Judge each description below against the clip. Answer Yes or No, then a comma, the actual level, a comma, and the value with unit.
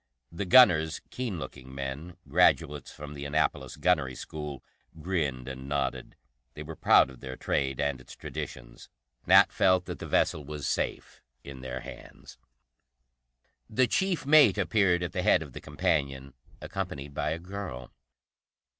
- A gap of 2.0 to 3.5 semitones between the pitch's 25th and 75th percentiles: No, average, 4.9 semitones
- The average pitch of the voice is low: Yes, very low, 75 Hz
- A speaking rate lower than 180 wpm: Yes, average, 150 wpm